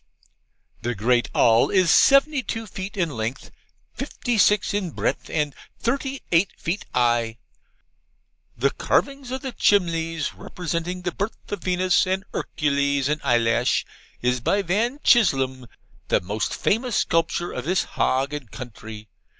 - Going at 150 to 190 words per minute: No, average, 140 wpm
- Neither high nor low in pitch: Yes, medium, 165 Hz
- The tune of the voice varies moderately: No, wide, 8.2 semitones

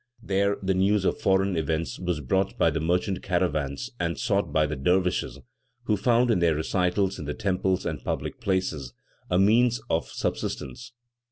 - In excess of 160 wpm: Yes, average, 170 wpm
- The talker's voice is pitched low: Yes, very low, 90 Hz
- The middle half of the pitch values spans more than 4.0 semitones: No, average, 3.7 semitones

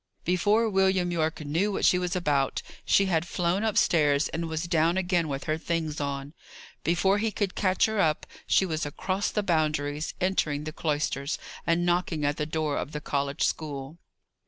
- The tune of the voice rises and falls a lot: No, average, 3.6 semitones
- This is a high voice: No, medium, 165 Hz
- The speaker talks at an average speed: Yes, average, 180 wpm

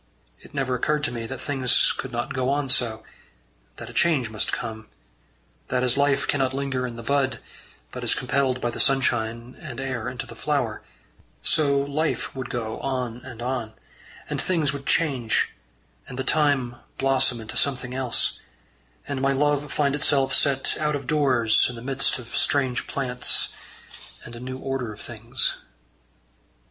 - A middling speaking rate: Yes, average, 170 wpm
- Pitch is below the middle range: Yes, low, 130 Hz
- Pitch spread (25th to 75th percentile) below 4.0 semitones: Yes, narrow, 2.6 semitones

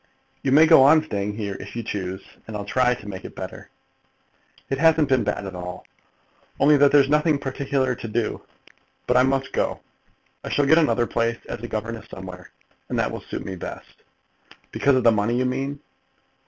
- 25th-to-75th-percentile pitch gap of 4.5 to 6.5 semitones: Yes, average, 5.0 semitones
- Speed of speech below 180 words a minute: No, average, 195 wpm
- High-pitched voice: No, low, 125 Hz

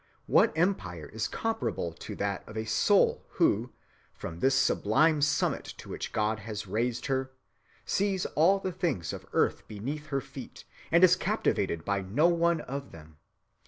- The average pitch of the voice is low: Yes, low, 130 Hz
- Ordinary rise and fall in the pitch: No, wide, 8.5 semitones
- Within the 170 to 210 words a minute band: No, average, 160 wpm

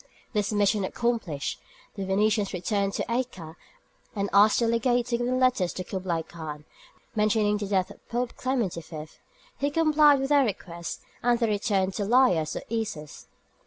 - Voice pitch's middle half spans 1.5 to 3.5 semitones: No, average, 4.5 semitones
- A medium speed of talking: Yes, average, 165 wpm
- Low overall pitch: No, high, 210 Hz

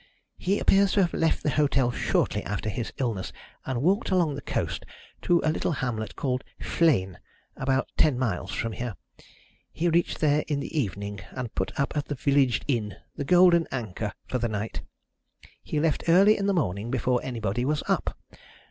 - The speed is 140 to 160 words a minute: No, average, 180 wpm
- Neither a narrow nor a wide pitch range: No, wide, 5.9 semitones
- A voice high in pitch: No, low, 135 Hz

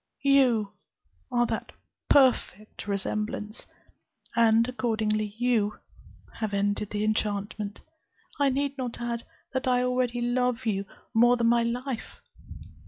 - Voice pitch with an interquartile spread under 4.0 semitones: Yes, average, 2.8 semitones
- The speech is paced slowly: Yes, slow, 115 wpm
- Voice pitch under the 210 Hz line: No, high, 235 Hz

